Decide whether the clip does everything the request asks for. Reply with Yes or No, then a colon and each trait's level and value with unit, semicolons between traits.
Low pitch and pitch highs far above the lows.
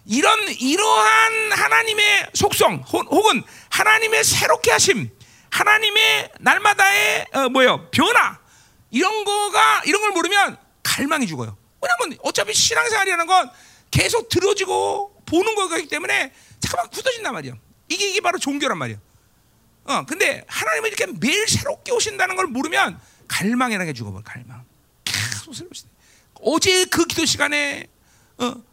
No: very high, 370 Hz; wide, 8.4 semitones